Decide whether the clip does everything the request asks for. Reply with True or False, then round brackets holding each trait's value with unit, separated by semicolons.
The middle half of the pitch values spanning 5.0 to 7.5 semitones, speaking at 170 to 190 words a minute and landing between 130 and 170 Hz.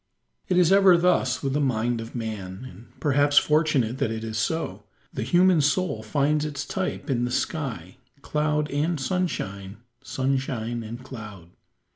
False (5.3 semitones; 155 wpm; 135 Hz)